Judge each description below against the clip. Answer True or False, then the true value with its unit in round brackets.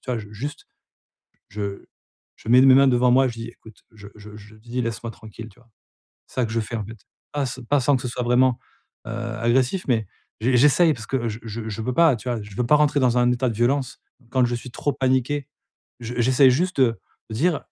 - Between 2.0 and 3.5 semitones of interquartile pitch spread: True (2.5 semitones)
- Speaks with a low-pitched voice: True (120 Hz)